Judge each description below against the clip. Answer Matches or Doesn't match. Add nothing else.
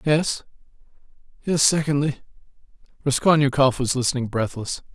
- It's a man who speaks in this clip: Matches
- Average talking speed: Doesn't match